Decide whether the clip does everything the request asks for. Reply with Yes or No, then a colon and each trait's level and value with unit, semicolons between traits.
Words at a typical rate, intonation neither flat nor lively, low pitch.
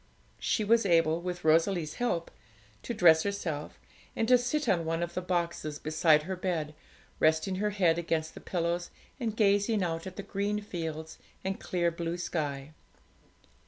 No: average, 160 wpm; average, 3.7 semitones; medium, 175 Hz